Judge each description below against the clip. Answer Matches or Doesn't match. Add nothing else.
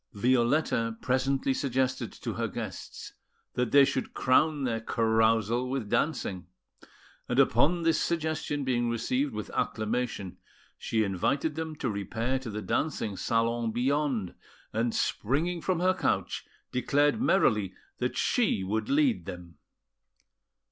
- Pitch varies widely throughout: Doesn't match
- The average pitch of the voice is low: Matches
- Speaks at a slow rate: Matches